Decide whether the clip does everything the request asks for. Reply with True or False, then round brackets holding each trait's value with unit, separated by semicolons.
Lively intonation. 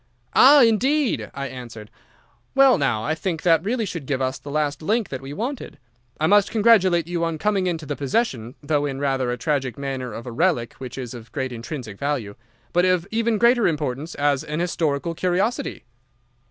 True (6.3 semitones)